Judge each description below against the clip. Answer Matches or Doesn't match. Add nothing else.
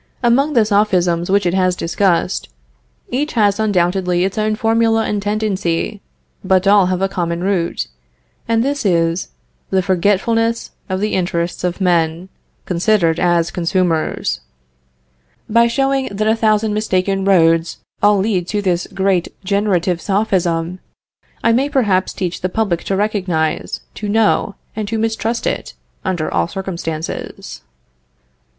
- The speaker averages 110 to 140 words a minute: Matches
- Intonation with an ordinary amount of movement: Matches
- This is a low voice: Doesn't match